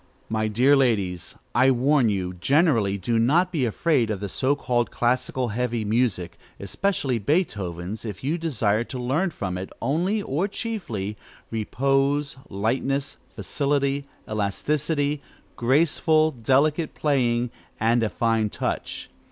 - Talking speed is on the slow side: Yes, slow, 125 wpm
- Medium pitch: No, low, 125 Hz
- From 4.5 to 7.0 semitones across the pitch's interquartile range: Yes, average, 5.0 semitones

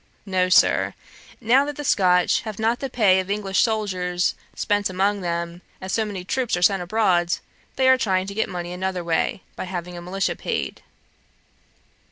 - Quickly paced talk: No, average, 180 wpm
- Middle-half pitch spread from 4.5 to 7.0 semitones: No, average, 3.3 semitones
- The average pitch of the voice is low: No, high, 190 Hz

